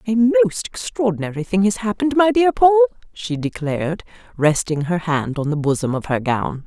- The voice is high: No, medium, 180 Hz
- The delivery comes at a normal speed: Yes, average, 180 wpm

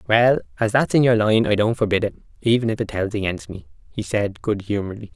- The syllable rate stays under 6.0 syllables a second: No, 6.1 syllables/s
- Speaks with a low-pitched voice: Yes, low, 105 Hz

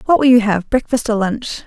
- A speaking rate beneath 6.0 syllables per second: Yes, 5.4 syllables/s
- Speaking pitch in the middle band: No, high, 230 Hz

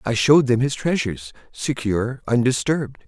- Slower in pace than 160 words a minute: Yes, slow, 135 wpm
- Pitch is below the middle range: Yes, low, 125 Hz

